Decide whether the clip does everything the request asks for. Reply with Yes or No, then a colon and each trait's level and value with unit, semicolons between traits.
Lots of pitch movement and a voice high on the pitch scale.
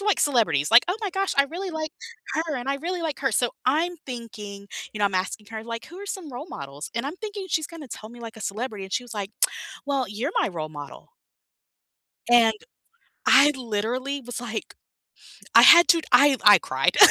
Yes: wide, 6.9 semitones; high, 245 Hz